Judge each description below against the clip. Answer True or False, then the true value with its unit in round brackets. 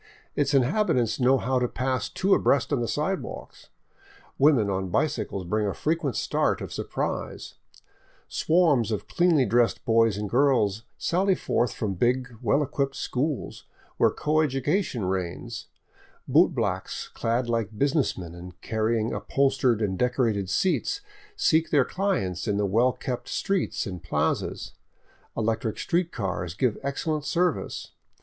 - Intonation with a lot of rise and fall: True (5.7 semitones)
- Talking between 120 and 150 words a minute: True (135 wpm)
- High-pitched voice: False (125 Hz)